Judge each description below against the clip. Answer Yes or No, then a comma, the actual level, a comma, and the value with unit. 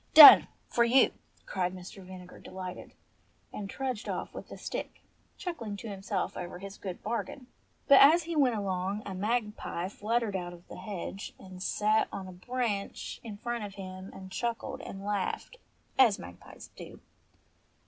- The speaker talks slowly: No, average, 160 wpm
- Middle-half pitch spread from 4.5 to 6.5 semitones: No, average, 3.9 semitones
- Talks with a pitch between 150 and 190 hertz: No, high, 200 Hz